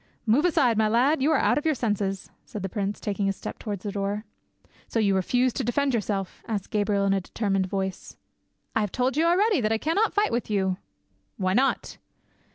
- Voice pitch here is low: No, high, 215 Hz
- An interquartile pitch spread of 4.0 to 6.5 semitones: Yes, average, 4.6 semitones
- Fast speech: Yes, fast, 210 wpm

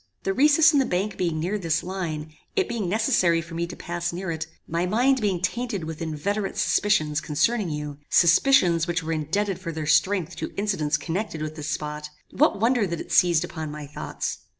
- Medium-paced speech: Yes, average, 195 wpm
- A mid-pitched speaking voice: Yes, medium, 175 Hz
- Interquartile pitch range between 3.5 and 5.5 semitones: Yes, average, 4.7 semitones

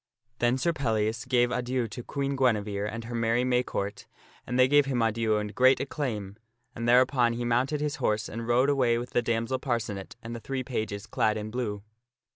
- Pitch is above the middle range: No, low, 120 Hz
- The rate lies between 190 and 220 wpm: Yes, average, 200 wpm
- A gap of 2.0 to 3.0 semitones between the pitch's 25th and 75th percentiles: Yes, average, 2.7 semitones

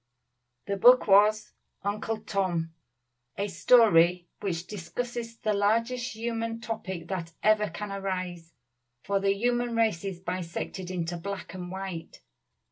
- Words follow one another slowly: Yes, slow, 125 wpm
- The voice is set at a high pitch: Yes, high, 200 Hz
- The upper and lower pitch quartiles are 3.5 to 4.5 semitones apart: Yes, average, 3.8 semitones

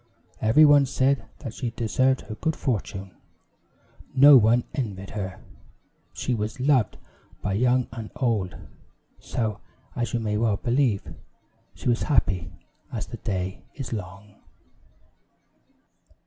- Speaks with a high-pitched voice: No, low, 115 Hz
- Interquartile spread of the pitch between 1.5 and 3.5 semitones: No, average, 4.2 semitones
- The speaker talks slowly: Yes, slow, 125 wpm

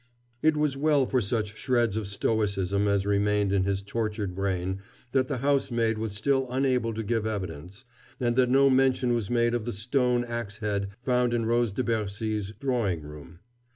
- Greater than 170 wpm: Yes, average, 180 wpm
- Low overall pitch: Yes, low, 115 Hz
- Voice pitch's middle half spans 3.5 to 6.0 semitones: Yes, average, 3.8 semitones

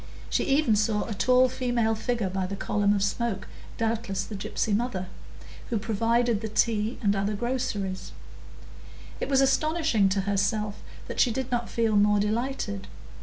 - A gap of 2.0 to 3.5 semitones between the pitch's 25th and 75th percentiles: Yes, average, 3.1 semitones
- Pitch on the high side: Yes, high, 220 Hz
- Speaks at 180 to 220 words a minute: No, average, 160 wpm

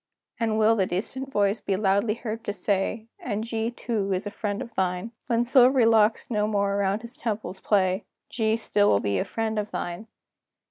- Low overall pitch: No, high, 215 Hz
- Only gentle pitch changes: Yes, narrow, 2.3 semitones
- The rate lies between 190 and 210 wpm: Yes, average, 195 wpm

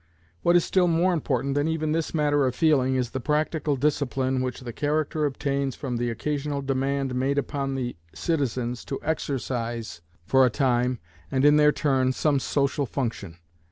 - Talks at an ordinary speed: Yes, average, 170 wpm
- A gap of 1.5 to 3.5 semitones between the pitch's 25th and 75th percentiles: Yes, average, 2.7 semitones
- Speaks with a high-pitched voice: No, low, 135 Hz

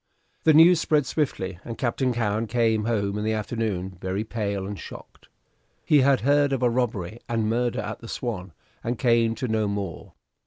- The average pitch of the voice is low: Yes, low, 115 Hz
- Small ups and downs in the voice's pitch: No, average, 3.3 semitones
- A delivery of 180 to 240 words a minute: Yes, average, 185 wpm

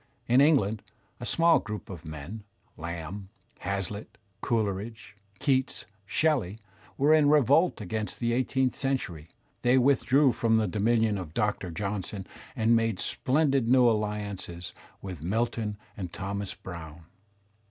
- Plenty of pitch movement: No, average, 4.9 semitones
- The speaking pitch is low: Yes, low, 105 Hz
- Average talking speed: No, slow, 125 wpm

